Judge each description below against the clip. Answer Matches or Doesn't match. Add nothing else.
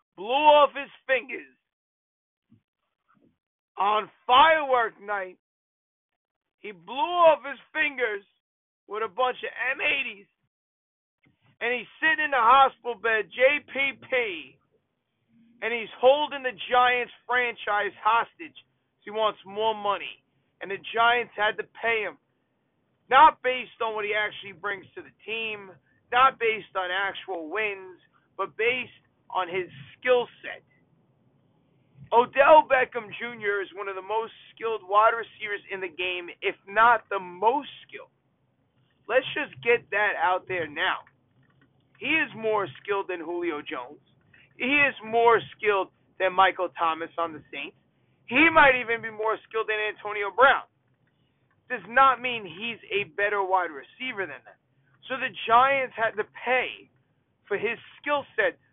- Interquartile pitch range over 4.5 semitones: Matches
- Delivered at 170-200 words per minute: Doesn't match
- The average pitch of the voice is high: Matches